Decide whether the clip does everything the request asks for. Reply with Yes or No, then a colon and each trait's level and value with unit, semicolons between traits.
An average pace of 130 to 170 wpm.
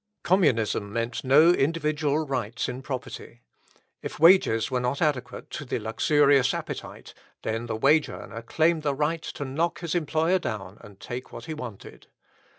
Yes: average, 155 wpm